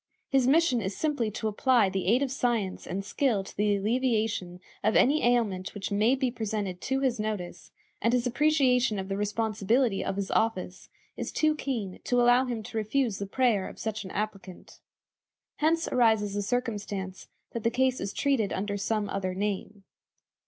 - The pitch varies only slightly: No, average, 3.9 semitones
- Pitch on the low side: No, high, 220 Hz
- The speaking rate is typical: Yes, average, 180 wpm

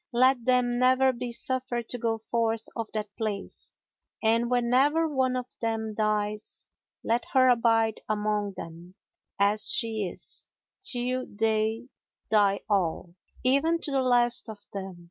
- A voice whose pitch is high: Yes, high, 230 Hz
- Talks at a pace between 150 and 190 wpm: No, average, 140 wpm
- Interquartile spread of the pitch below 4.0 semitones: Yes, average, 3.0 semitones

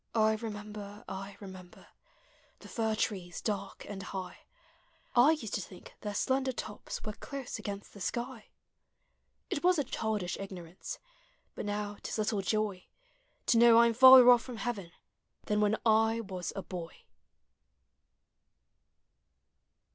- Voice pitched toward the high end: Yes, high, 210 Hz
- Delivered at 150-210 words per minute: No, average, 140 wpm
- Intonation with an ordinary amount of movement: Yes, average, 3.0 semitones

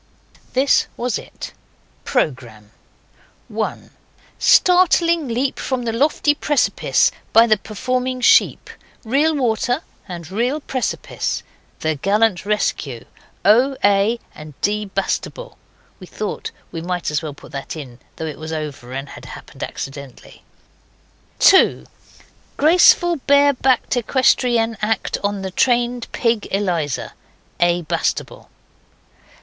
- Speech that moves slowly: Yes, slow, 120 wpm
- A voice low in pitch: No, high, 220 Hz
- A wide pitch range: Yes, wide, 7.5 semitones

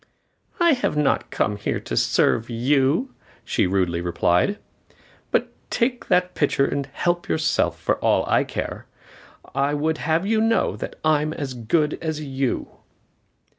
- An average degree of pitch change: Yes, average, 5.0 semitones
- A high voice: No, medium, 150 Hz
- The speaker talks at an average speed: Yes, average, 150 wpm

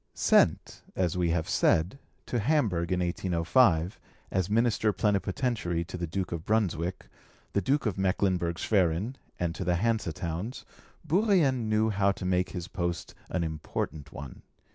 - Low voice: Yes, very low, 95 Hz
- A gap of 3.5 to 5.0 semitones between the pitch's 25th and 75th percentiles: Yes, average, 4.3 semitones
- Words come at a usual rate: Yes, average, 150 wpm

